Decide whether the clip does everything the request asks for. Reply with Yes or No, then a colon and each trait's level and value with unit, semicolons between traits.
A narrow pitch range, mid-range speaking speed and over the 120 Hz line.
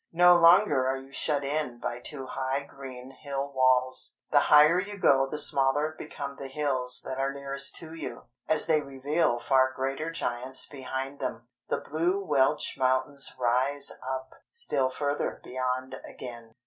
Yes: narrow, 2.3 semitones; average, 160 wpm; low, 135 Hz